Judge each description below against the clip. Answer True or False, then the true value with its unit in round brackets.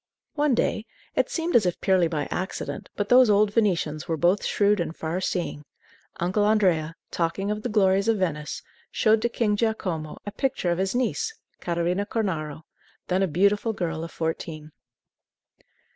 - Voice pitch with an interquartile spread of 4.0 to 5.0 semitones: True (4.3 semitones)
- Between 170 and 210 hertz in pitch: True (190 Hz)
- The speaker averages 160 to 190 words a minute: True (165 wpm)